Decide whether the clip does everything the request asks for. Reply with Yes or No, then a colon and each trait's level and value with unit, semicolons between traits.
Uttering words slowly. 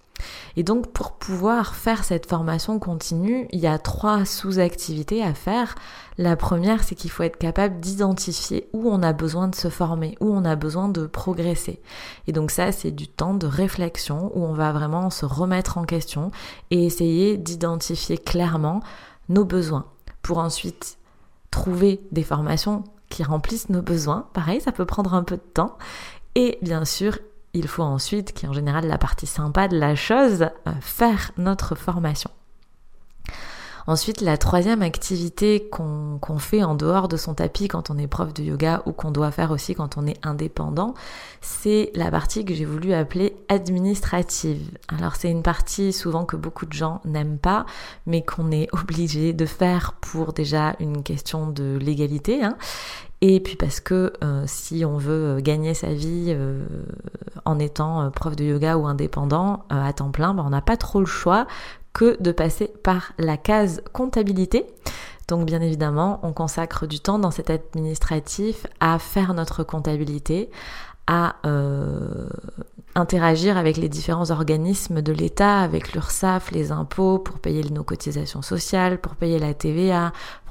No: average, 170 wpm